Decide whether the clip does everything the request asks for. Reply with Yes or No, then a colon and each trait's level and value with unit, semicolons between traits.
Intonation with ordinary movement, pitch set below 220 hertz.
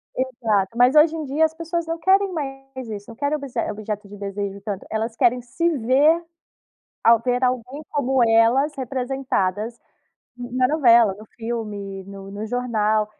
No: average, 4.2 semitones; high, 245 Hz